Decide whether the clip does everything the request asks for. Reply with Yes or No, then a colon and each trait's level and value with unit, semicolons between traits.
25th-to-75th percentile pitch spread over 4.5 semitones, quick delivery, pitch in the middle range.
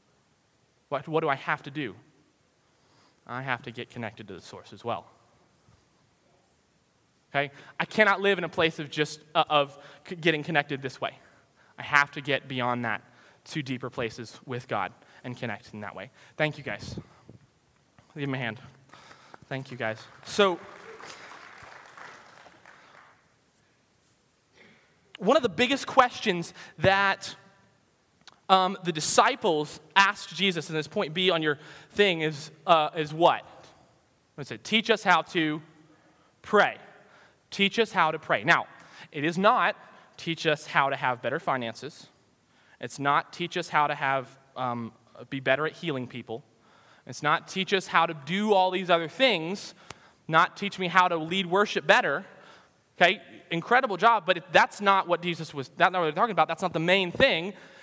No: average, 5.2 semitones; average, 165 wpm; medium, 155 Hz